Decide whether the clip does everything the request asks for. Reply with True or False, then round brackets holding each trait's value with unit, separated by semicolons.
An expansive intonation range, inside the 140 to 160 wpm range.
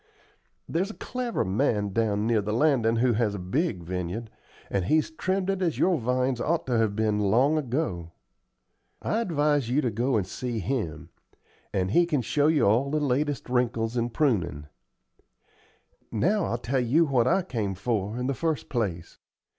False (6.0 semitones; 175 wpm)